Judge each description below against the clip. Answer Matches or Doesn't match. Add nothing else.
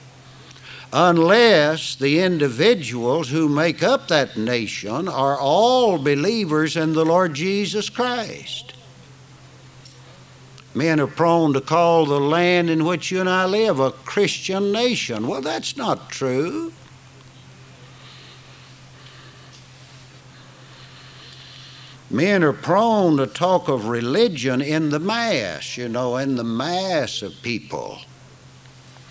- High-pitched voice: Doesn't match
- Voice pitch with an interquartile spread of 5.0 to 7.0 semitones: Doesn't match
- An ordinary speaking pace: Doesn't match